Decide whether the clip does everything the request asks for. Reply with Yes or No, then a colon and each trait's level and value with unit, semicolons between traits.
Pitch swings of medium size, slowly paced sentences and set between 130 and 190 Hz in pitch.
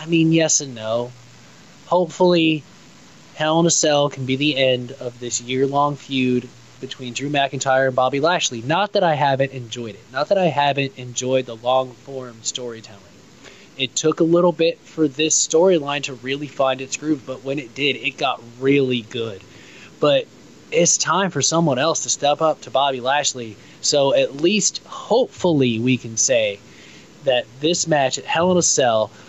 No: average, 3.9 semitones; average, 180 wpm; low, 135 Hz